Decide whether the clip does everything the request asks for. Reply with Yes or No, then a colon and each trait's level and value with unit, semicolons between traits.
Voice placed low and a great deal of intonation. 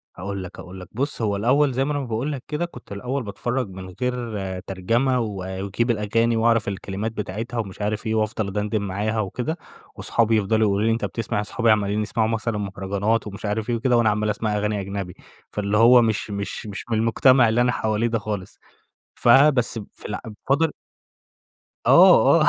No: low, 110 Hz; average, 2.8 semitones